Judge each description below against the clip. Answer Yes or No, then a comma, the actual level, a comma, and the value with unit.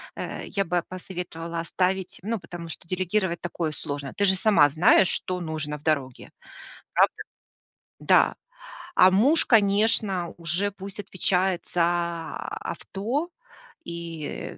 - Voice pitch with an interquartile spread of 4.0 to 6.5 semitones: No, average, 2.8 semitones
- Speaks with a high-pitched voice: No, medium, 180 Hz